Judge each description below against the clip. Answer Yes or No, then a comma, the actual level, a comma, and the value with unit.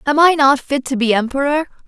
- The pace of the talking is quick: Yes, fast, 225 wpm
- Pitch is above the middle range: Yes, very high, 275 Hz